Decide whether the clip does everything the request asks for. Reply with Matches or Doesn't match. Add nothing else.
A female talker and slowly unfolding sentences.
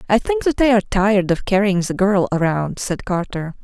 Doesn't match